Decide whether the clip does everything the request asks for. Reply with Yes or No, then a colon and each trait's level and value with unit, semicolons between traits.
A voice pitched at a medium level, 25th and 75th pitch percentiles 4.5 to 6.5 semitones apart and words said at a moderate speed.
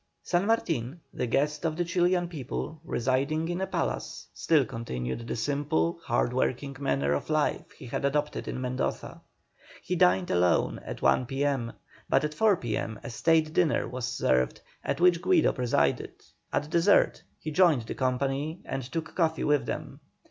Yes: medium, 145 Hz; average, 5.1 semitones; average, 165 wpm